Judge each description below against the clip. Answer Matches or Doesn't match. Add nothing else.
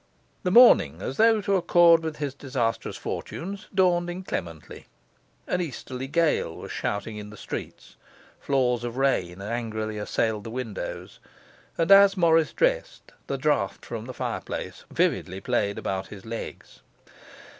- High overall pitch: Doesn't match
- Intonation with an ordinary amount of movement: Doesn't match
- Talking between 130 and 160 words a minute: Matches